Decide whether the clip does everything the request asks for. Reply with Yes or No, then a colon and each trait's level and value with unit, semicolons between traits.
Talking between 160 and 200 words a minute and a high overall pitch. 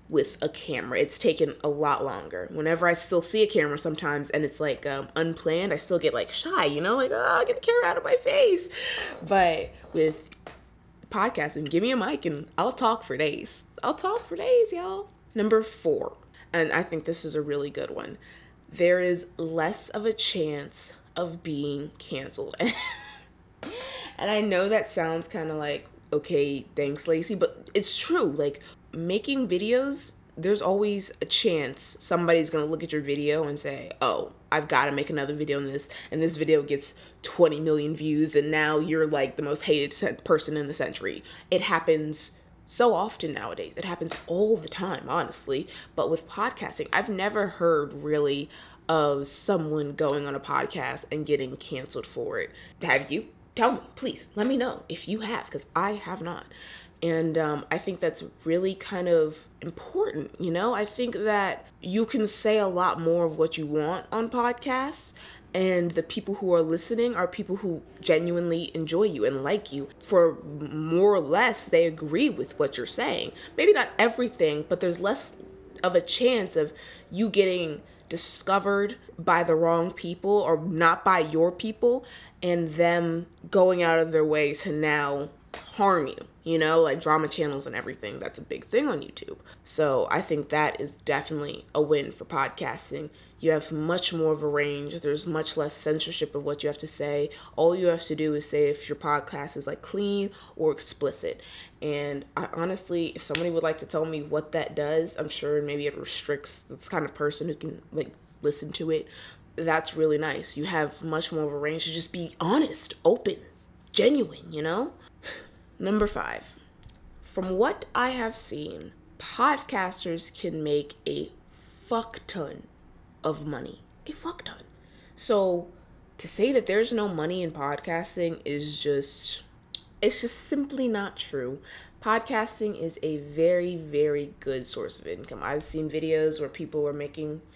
No: average, 180 wpm; medium, 165 Hz